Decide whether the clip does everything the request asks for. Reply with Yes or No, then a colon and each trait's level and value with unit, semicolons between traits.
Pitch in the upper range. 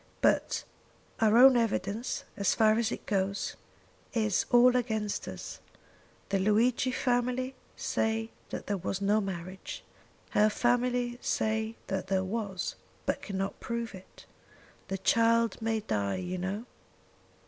Yes: high, 220 Hz